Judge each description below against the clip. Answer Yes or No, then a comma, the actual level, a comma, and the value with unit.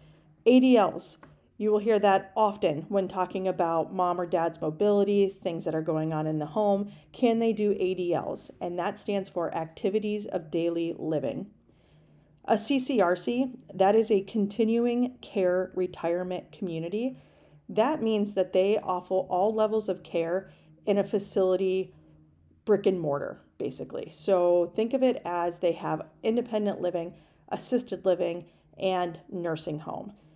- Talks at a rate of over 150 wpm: No, average, 140 wpm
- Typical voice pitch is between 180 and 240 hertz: Yes, medium, 185 Hz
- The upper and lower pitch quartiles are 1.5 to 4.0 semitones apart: Yes, average, 3.7 semitones